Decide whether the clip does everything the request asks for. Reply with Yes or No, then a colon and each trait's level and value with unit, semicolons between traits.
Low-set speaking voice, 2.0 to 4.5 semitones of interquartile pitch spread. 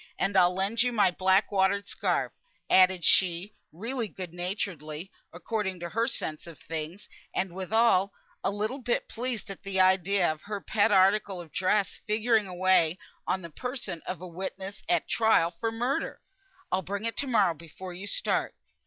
No: high, 190 Hz; average, 3.2 semitones